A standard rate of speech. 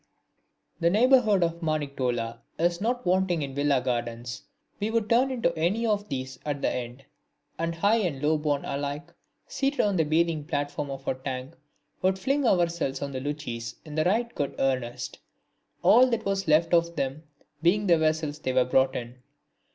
Yes: average, 175 wpm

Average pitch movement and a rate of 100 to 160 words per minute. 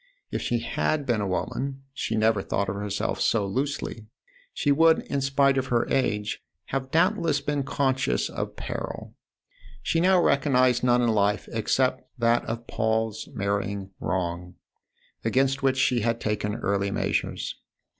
Yes: average, 4.7 semitones; average, 150 wpm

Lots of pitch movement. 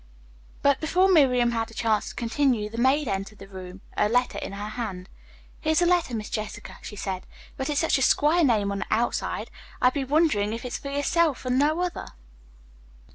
Yes: wide, 5.7 semitones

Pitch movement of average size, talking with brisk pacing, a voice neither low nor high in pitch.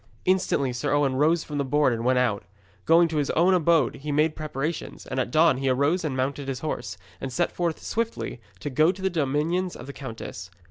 Yes: average, 4.1 semitones; fast, 220 wpm; medium, 145 Hz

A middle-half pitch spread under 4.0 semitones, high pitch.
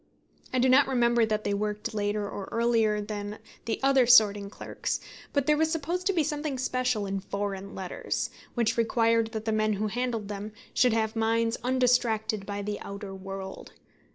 Yes: average, 3.3 semitones; high, 220 Hz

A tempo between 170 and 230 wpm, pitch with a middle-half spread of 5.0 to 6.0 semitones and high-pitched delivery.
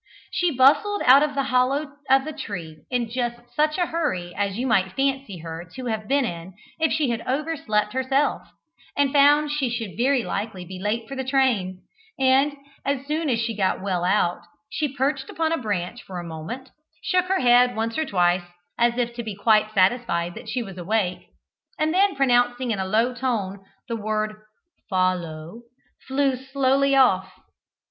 Yes: average, 180 wpm; wide, 5.5 semitones; high, 245 Hz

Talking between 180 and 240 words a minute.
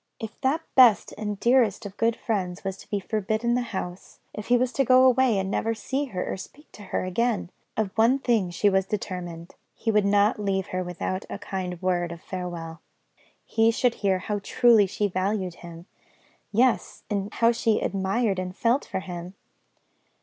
Yes: average, 190 wpm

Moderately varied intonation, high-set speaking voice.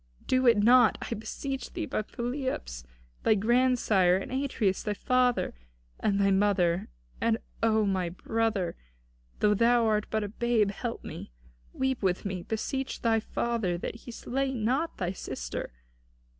Yes: average, 3.8 semitones; high, 220 Hz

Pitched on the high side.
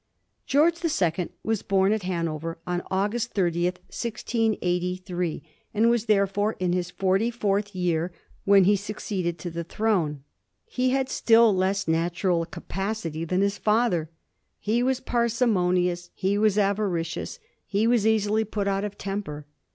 Yes: high, 195 Hz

